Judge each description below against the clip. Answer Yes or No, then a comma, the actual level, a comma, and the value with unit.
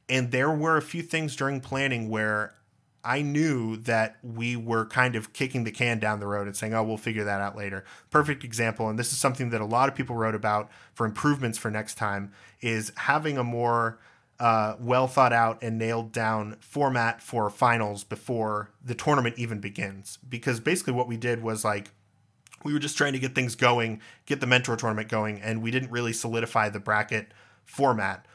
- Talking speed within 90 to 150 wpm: No, average, 200 wpm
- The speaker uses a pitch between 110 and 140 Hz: Yes, low, 115 Hz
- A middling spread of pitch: Yes, average, 3.0 semitones